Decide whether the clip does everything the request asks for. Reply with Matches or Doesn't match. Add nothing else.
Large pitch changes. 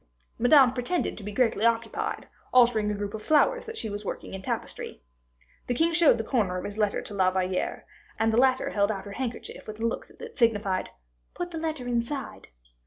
Doesn't match